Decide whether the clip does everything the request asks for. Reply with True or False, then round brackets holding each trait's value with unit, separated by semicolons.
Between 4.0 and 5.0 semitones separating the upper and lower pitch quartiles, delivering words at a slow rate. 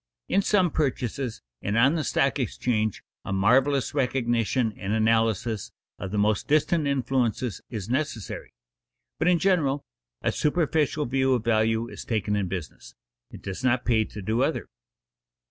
False (4.4 semitones; 150 wpm)